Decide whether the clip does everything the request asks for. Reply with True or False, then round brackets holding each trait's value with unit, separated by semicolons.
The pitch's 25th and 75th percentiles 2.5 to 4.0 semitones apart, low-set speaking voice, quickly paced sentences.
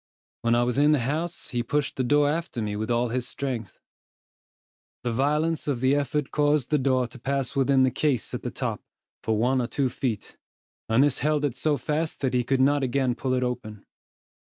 True (3.2 semitones; 130 Hz; 210 wpm)